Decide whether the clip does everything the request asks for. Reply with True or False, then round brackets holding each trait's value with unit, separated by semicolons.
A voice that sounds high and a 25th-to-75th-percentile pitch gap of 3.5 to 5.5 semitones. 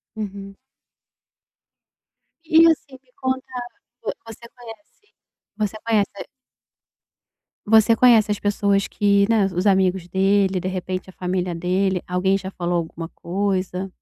False (195 Hz; 3.0 semitones)